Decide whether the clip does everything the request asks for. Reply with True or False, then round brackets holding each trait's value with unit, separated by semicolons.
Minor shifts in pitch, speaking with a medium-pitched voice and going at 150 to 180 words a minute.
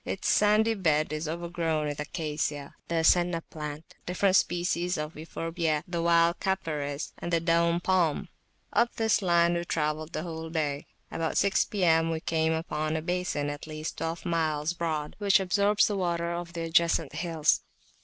True (2.1 semitones; 165 Hz; 165 wpm)